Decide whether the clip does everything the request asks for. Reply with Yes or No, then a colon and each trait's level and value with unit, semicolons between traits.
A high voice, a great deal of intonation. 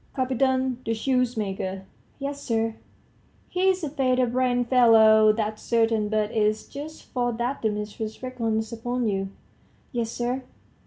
No: high, 235 Hz; average, 2.8 semitones